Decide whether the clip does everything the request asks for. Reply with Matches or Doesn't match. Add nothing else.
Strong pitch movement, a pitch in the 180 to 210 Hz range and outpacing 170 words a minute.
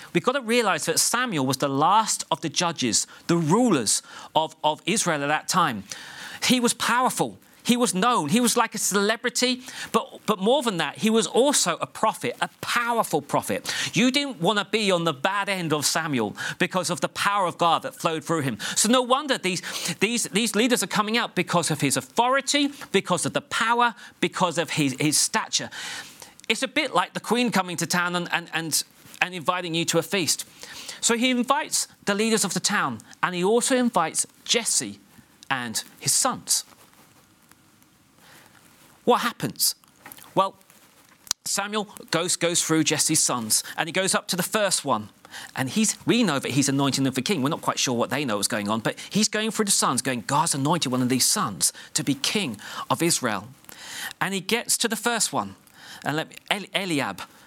Matches